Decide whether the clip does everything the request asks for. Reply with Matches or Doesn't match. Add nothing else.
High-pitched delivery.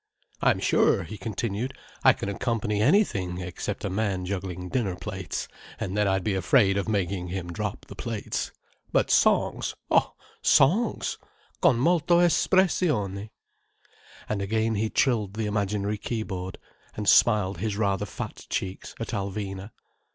Doesn't match